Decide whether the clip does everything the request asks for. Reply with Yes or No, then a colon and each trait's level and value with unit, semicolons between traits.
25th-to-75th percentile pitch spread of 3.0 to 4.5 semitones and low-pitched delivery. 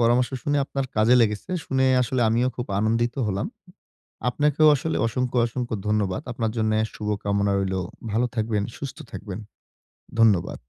Yes: average, 3.3 semitones; low, 115 Hz